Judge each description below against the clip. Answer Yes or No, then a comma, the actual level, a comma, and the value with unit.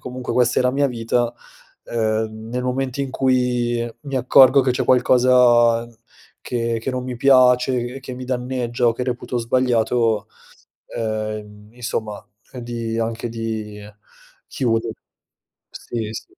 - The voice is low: Yes, low, 120 Hz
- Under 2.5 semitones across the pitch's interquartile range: Yes, narrow, 1.9 semitones